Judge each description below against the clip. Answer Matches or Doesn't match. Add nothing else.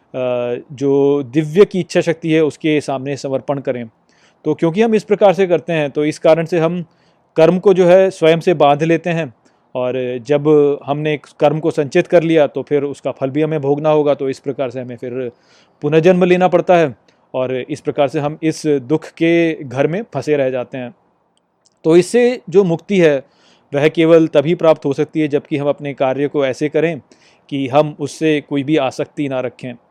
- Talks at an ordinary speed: Doesn't match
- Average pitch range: Matches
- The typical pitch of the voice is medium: Matches